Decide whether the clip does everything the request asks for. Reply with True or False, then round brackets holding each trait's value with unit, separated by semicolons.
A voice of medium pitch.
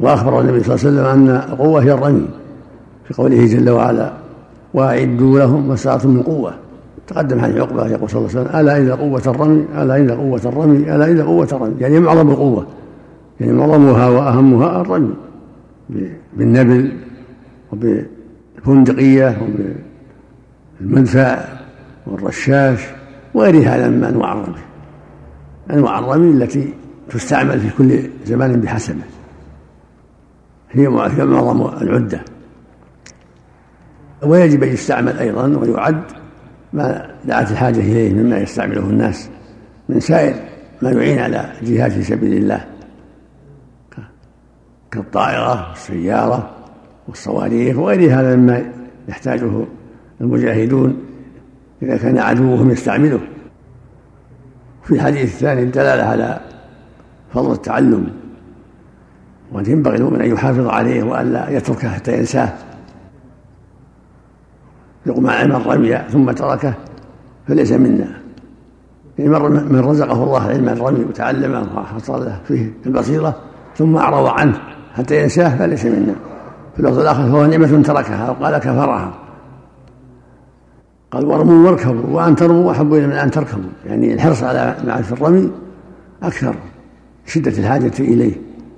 False (130 Hz)